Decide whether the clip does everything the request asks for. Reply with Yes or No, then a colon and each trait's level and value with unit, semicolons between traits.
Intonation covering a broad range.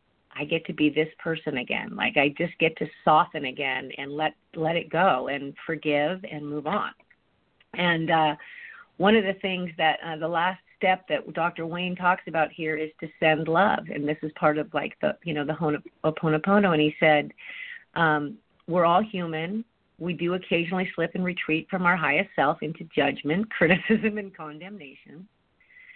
No: average, 3.2 semitones